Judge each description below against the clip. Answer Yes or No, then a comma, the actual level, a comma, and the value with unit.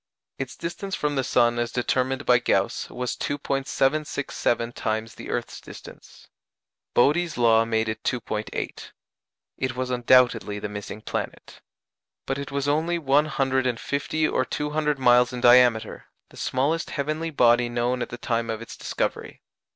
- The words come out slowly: No, average, 155 wpm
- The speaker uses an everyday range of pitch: Yes, average, 3.2 semitones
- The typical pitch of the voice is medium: No, low, 125 Hz